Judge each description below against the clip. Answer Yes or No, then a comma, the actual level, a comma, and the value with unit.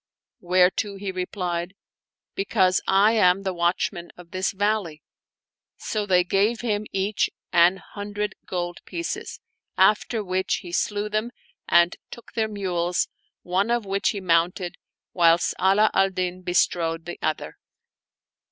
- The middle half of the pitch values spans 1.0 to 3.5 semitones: Yes, narrow, 2.6 semitones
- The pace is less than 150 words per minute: Yes, average, 140 wpm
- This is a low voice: No, high, 190 Hz